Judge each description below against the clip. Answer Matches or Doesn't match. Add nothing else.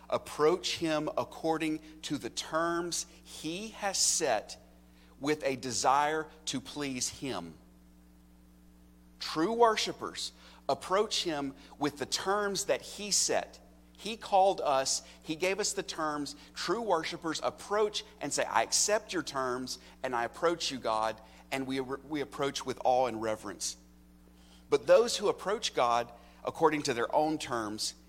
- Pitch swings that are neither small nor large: Doesn't match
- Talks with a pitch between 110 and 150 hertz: Matches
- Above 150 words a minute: Doesn't match